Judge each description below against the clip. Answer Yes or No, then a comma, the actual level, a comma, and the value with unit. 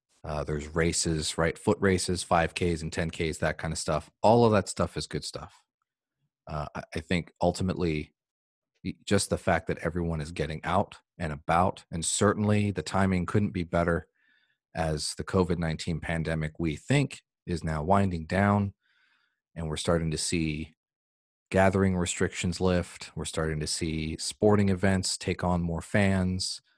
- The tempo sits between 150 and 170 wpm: Yes, average, 155 wpm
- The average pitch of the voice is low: Yes, very low, 85 Hz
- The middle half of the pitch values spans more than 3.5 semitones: No, average, 2.9 semitones